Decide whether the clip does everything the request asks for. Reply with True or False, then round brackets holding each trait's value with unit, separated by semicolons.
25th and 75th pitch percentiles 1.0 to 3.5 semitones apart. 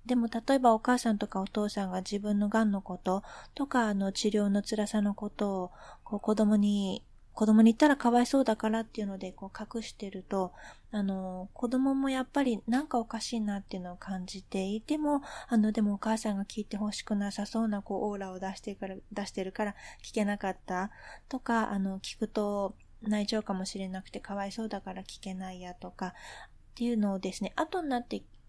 True (2.6 semitones)